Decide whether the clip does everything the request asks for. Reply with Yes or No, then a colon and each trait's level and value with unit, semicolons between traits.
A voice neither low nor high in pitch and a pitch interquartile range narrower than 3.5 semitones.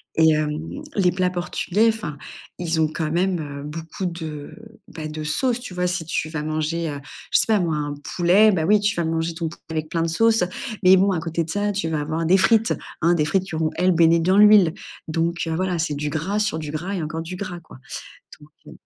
Yes: medium, 165 Hz; average, 3.1 semitones